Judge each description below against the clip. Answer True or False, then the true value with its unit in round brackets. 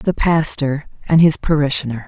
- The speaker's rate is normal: True (145 wpm)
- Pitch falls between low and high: True (150 Hz)